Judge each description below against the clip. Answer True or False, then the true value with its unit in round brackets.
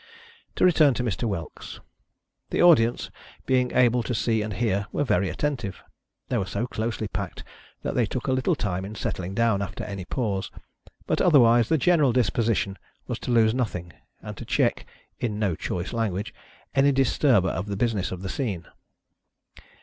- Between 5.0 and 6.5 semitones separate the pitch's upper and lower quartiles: False (4.3 semitones)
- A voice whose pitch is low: True (115 Hz)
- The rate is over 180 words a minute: False (175 wpm)